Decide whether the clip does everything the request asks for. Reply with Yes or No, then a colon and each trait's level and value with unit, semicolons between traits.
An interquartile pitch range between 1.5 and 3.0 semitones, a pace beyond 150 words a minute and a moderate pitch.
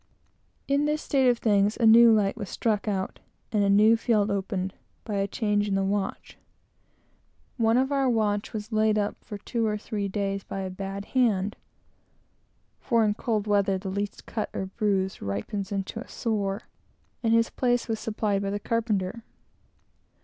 No: narrow, 2.5 semitones; average, 175 wpm; high, 210 Hz